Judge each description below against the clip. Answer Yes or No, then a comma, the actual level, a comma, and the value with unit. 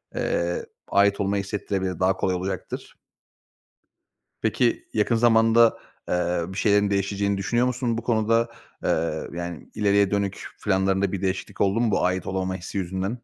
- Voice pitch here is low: Yes, low, 100 Hz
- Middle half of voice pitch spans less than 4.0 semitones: Yes, average, 2.9 semitones